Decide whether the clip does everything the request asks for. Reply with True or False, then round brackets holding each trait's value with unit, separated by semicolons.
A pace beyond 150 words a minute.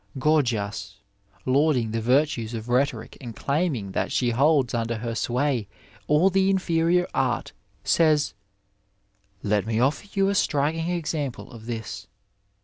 False (140 wpm)